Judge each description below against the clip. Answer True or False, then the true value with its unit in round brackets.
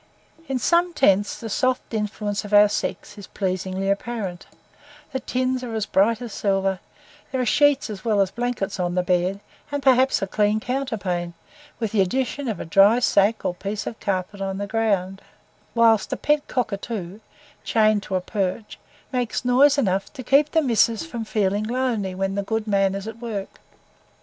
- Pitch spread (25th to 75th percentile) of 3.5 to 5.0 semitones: True (4.0 semitones)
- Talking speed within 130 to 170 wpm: False (180 wpm)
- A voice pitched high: True (215 Hz)